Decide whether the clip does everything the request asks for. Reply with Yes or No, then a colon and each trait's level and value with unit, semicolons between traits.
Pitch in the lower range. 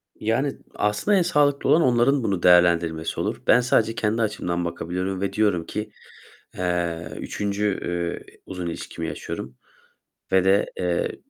Yes: very low, 95 Hz